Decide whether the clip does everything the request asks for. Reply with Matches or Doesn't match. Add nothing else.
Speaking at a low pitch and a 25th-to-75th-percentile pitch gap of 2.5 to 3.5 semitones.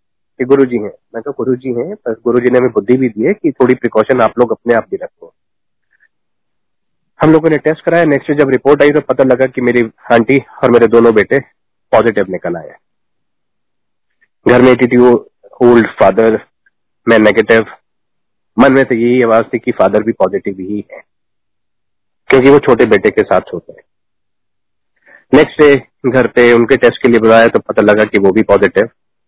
Matches